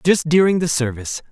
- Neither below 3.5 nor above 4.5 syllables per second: No, 6.0 syllables/s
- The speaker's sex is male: Yes, male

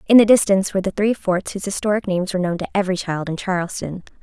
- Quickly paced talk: Yes, fast, 240 wpm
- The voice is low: No, high, 190 Hz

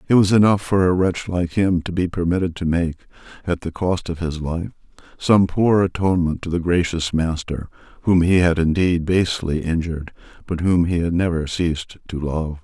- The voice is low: Yes, very low, 85 Hz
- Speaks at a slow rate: No, average, 190 wpm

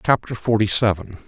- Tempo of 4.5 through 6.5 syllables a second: Yes, 5.7 syllables/s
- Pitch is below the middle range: Yes, low, 110 Hz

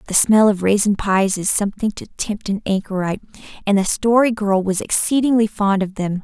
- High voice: Yes, high, 205 Hz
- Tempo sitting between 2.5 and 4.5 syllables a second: No, 5.4 syllables/s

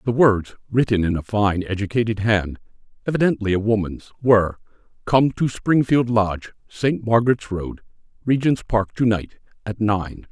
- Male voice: Yes, male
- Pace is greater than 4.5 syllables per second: Yes, 4.9 syllables/s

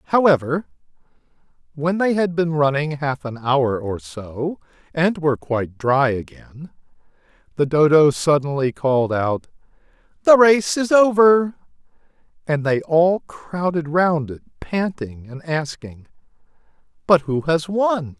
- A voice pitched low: No, medium, 155 Hz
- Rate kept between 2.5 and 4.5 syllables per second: Yes, 4.1 syllables/s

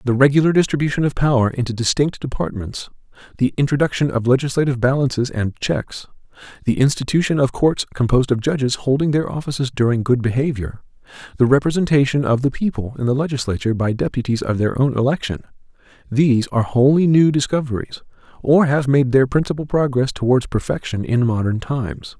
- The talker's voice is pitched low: Yes, low, 130 Hz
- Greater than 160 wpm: No, average, 155 wpm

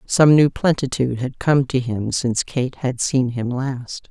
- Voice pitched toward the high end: No, low, 130 Hz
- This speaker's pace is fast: No, average, 190 wpm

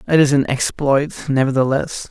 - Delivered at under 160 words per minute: Yes, average, 140 wpm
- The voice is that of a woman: No, male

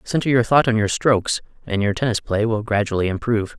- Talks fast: Yes, fast, 215 wpm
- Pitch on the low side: Yes, low, 110 Hz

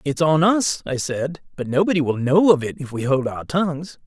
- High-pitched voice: No, medium, 150 Hz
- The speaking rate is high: Yes, fast, 235 wpm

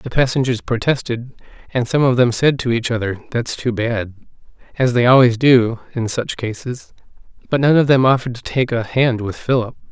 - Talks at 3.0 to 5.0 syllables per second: No, 5.3 syllables/s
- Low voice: Yes, low, 120 Hz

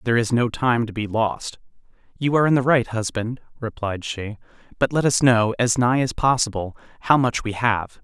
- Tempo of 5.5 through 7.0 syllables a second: No, 5.2 syllables/s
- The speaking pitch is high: No, low, 115 Hz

